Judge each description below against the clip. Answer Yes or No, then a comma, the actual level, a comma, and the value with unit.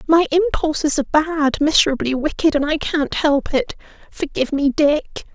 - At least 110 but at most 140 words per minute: Yes, slow, 135 wpm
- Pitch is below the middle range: No, very high, 300 Hz